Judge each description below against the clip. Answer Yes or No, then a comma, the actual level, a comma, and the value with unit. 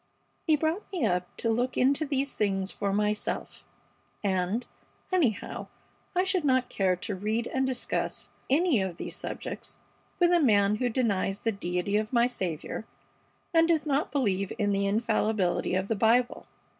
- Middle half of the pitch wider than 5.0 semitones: Yes, wide, 5.4 semitones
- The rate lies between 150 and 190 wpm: Yes, average, 160 wpm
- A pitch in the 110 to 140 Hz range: No, high, 225 Hz